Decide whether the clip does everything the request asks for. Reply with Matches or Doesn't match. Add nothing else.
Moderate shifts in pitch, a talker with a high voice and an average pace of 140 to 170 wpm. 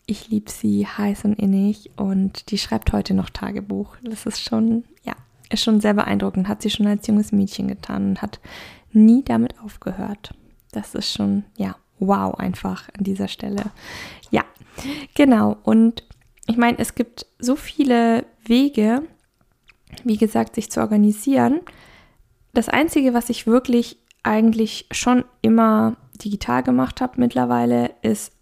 Matches